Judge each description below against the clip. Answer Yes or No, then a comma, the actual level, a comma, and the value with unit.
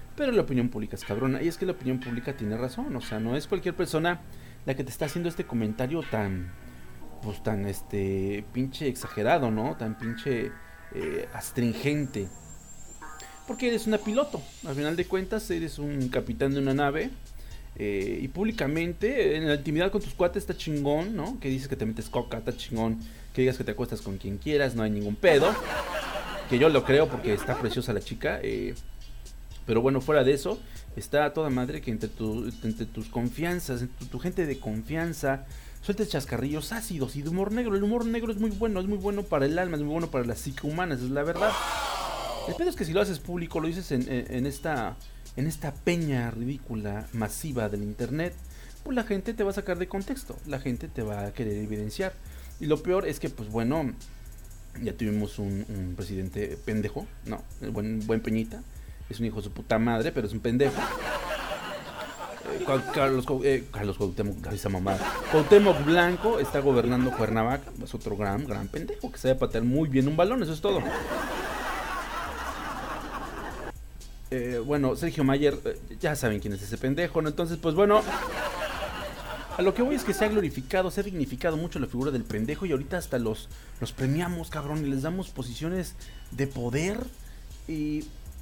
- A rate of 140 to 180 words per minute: No, average, 190 wpm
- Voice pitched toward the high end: No, low, 135 Hz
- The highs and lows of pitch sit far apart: Yes, wide, 7.1 semitones